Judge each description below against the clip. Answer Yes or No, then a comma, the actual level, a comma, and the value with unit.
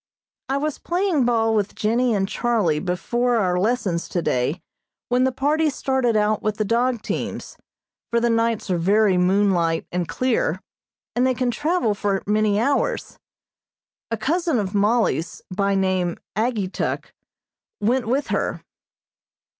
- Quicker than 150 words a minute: No, average, 140 wpm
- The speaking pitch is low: No, high, 220 Hz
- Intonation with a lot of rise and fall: No, average, 4.6 semitones